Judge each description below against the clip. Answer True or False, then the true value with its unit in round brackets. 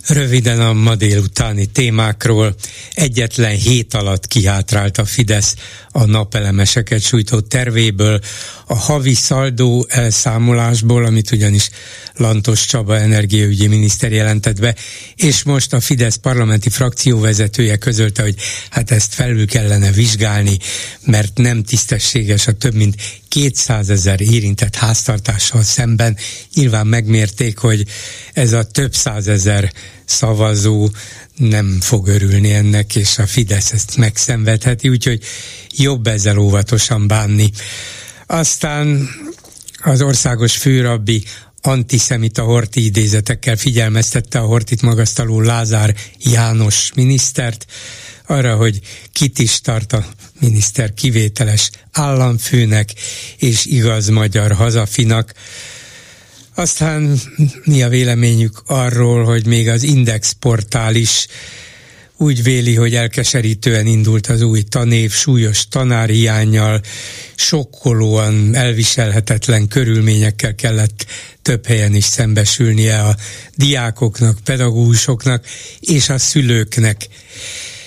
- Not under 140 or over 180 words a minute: False (105 wpm)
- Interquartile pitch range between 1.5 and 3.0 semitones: True (2.7 semitones)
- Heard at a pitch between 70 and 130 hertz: True (115 Hz)